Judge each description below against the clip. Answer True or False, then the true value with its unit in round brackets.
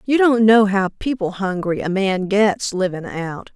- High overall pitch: True (200 Hz)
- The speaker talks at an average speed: True (185 wpm)